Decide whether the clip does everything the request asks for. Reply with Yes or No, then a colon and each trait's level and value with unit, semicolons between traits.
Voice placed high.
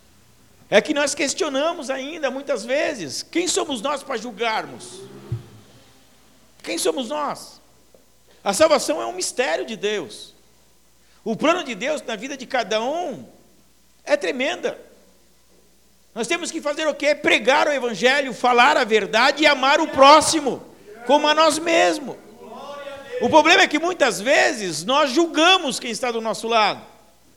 Yes: very high, 285 Hz